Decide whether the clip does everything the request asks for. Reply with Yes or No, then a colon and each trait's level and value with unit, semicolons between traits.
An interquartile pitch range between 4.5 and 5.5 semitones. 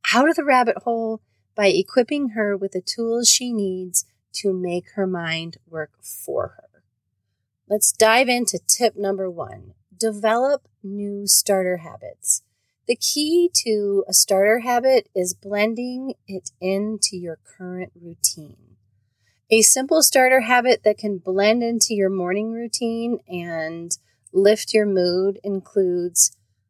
Yes: average, 5.2 semitones